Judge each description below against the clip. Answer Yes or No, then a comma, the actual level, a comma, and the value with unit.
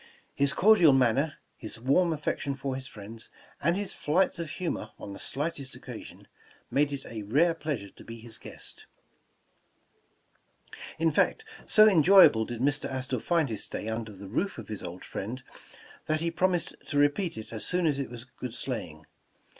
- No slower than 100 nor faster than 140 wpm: No, average, 180 wpm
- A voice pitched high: No, medium, 140 Hz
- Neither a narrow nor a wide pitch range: No, wide, 6.4 semitones